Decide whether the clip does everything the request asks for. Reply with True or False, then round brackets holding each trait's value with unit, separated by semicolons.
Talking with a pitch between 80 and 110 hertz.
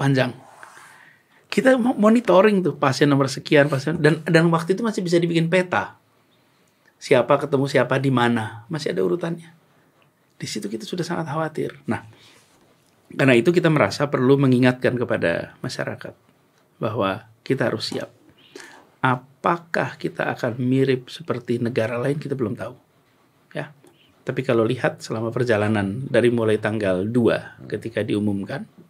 False (135 Hz)